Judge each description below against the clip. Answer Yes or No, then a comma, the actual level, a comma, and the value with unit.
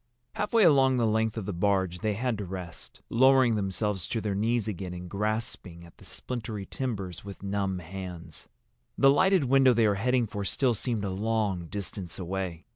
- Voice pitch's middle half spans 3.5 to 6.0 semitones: Yes, average, 4.0 semitones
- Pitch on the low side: Yes, low, 105 Hz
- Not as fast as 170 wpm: No, average, 185 wpm